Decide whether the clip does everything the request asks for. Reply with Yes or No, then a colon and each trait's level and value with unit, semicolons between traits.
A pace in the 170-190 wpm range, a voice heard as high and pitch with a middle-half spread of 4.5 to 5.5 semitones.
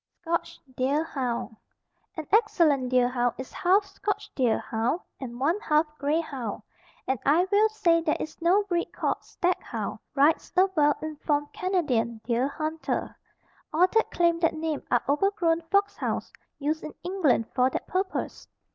No: average, 160 wpm; very high, 310 Hz; average, 5.2 semitones